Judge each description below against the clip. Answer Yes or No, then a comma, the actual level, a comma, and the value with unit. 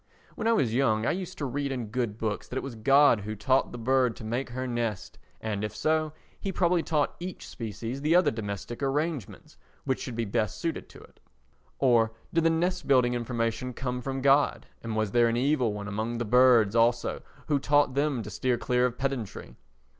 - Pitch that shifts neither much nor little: Yes, average, 3.7 semitones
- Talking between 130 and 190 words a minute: No, fast, 205 wpm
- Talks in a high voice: No, low, 125 Hz